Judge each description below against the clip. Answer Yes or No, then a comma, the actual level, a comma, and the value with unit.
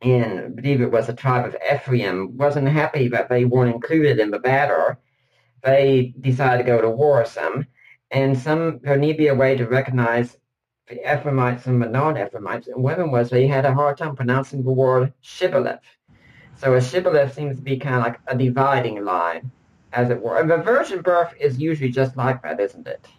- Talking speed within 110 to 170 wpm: No, average, 200 wpm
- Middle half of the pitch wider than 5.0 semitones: No, narrow, 2.5 semitones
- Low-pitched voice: Yes, low, 130 Hz